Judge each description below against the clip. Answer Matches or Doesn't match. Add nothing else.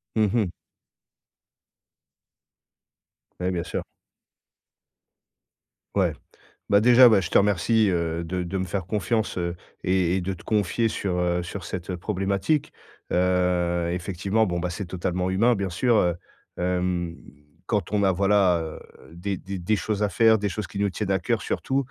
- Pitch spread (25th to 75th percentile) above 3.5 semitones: Doesn't match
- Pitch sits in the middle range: Doesn't match